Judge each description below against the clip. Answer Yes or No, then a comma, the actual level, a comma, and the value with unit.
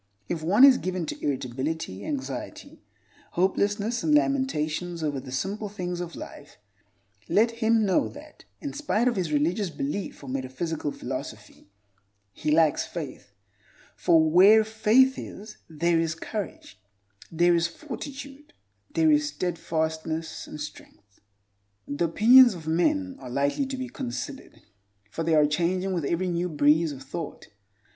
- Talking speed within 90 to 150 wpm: Yes, average, 140 wpm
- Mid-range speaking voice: Yes, medium, 170 Hz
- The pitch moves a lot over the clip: Yes, wide, 6.3 semitones